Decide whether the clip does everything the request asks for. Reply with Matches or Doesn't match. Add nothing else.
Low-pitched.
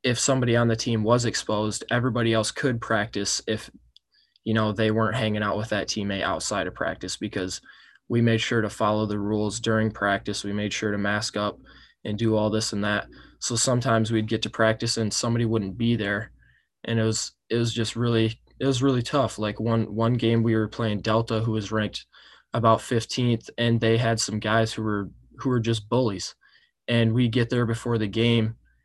Matches